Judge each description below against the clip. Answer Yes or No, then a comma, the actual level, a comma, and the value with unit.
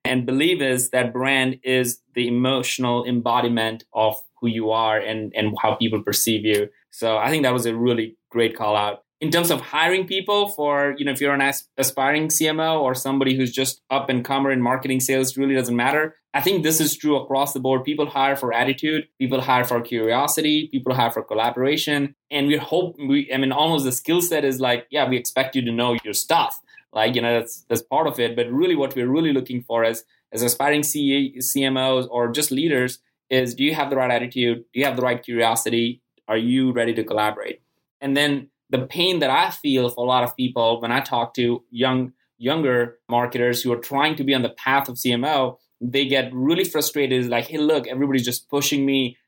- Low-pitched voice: Yes, low, 130 Hz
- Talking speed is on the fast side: Yes, fast, 215 wpm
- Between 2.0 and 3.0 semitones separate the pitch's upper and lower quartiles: Yes, narrow, 2.6 semitones